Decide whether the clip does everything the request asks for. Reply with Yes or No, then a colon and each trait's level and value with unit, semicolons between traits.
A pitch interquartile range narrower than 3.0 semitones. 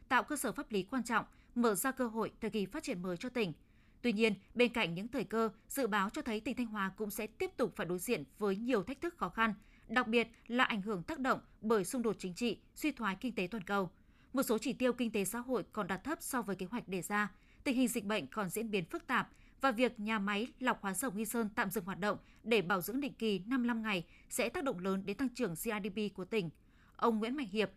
No: average, 3.3 semitones